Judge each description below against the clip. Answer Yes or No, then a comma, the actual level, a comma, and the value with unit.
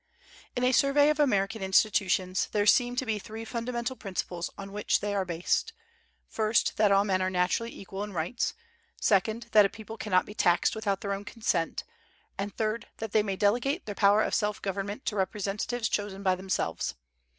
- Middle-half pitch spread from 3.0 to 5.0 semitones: No, narrow, 2.6 semitones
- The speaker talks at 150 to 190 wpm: Yes, average, 185 wpm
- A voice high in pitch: Yes, high, 205 Hz